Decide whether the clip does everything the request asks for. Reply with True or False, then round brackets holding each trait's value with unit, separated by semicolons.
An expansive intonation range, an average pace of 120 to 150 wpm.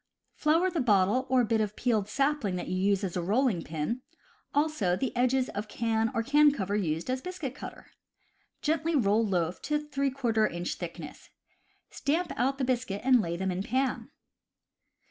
False (5.9 semitones; 170 wpm)